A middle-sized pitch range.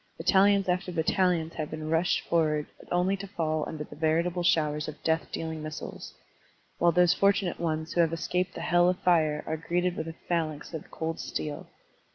No: narrow, 2.2 semitones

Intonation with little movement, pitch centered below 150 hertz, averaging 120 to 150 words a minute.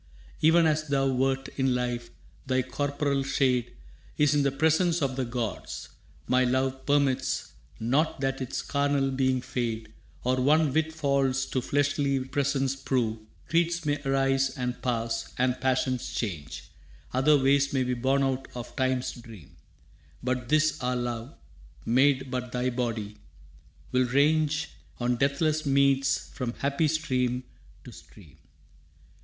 Yes: narrow, 2.2 semitones; low, 135 Hz; average, 140 wpm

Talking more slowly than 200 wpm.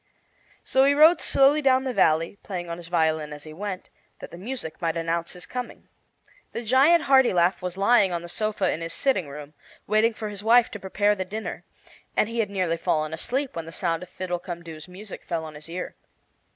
No: fast, 205 wpm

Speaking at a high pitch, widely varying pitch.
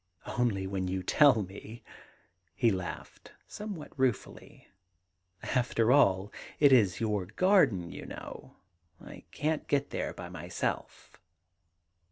No: low, 110 Hz; wide, 6.3 semitones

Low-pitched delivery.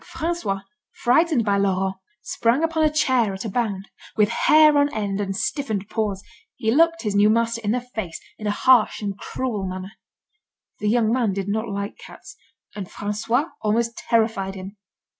No: high, 220 Hz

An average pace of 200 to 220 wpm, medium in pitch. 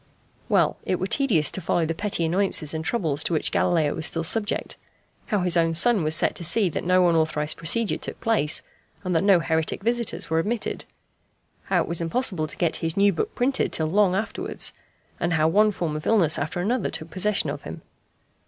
Yes: fast, 205 wpm; medium, 175 Hz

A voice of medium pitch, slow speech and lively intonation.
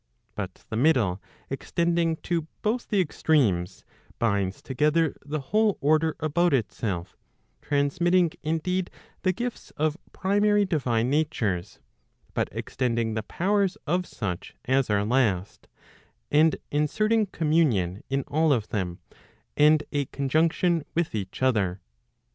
Yes: medium, 150 Hz; slow, 120 wpm; wide, 7.2 semitones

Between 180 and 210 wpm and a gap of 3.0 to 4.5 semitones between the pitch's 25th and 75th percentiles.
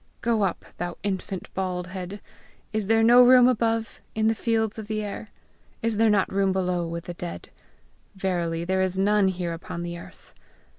Yes: average, 185 wpm; average, 3.6 semitones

